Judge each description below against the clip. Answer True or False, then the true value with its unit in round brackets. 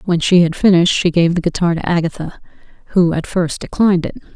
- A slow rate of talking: False (205 wpm)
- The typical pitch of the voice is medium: True (175 Hz)